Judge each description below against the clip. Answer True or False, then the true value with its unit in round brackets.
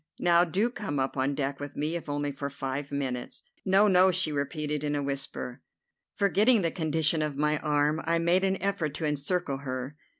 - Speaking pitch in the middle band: True (150 Hz)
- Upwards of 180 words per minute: True (195 wpm)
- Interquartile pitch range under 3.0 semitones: False (3.7 semitones)